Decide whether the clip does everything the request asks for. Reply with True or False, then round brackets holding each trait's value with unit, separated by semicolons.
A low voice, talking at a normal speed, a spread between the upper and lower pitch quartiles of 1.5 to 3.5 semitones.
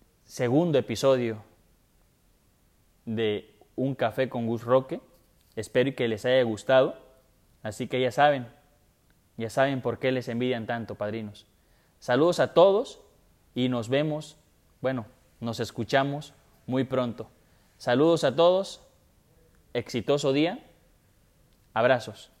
False (125 Hz; 115 wpm; 3.2 semitones)